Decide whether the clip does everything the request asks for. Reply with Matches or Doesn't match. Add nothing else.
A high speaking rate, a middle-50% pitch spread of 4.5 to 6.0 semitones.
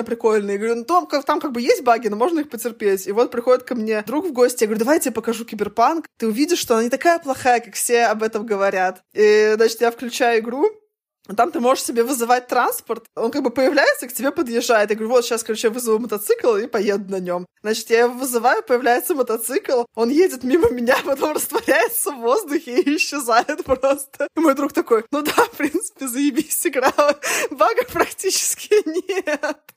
Matches